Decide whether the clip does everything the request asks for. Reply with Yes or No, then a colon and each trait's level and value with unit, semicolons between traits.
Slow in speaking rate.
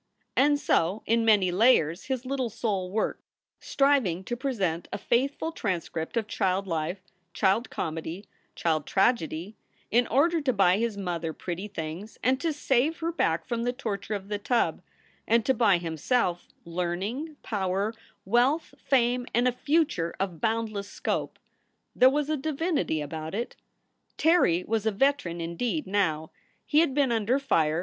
No: average, 155 wpm